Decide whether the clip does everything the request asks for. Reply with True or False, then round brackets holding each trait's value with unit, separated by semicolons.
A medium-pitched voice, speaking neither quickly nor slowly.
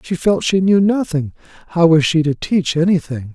True (170 Hz; 195 wpm)